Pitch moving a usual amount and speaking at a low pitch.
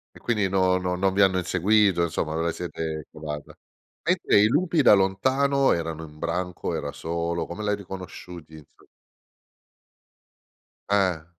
Yes: average, 3.5 semitones; very low, 90 Hz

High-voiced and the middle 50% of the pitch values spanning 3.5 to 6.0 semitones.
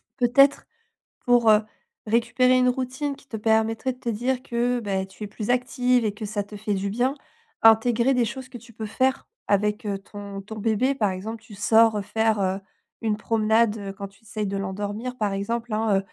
No: high, 220 Hz; average, 3.1 semitones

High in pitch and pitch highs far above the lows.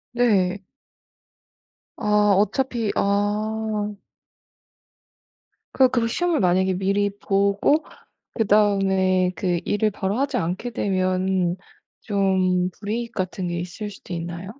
No: high, 200 Hz; narrow, 2.5 semitones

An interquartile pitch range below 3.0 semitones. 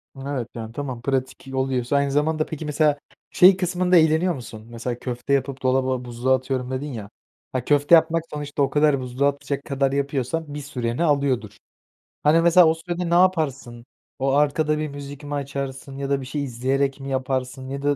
Yes: narrow, 2.4 semitones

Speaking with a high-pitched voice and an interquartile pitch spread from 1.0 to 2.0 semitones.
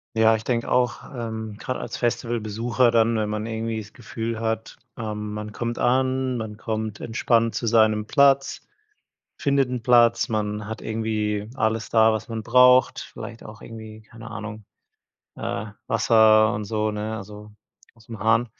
No: low, 110 Hz; narrow, 1.4 semitones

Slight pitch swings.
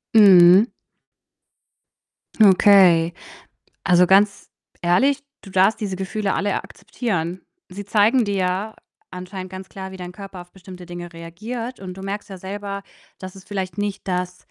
Yes: narrow, 2.1 semitones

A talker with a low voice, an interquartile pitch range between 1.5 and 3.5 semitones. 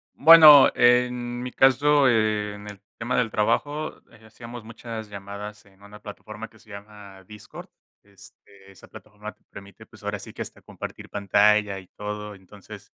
Yes: low, 105 Hz; average, 3.0 semitones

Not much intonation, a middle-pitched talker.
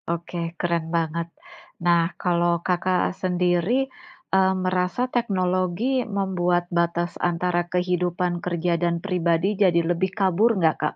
Yes: narrow, 1.3 semitones; medium, 180 Hz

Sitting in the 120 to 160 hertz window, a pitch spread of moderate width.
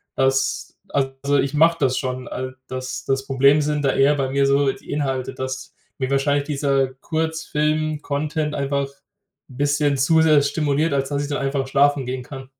No: medium, 140 Hz; narrow, 1.7 semitones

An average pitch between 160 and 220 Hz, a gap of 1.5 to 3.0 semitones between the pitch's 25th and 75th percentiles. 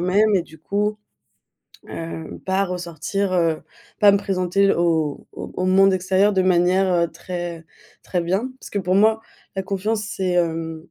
Yes: medium, 185 Hz; narrow, 2.4 semitones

